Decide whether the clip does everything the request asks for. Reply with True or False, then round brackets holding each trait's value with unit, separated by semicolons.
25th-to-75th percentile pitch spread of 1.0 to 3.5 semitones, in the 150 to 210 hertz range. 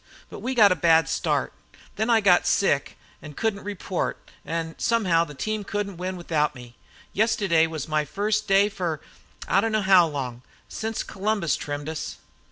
False (4.6 semitones; 185 Hz)